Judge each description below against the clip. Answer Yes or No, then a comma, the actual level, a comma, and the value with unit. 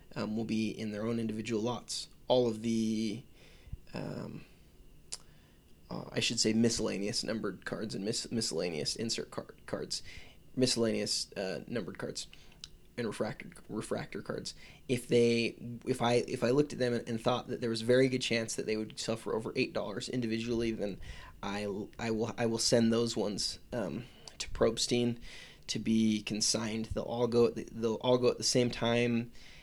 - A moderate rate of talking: Yes, average, 175 wpm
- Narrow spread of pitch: Yes, narrow, 1.6 semitones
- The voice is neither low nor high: No, low, 115 Hz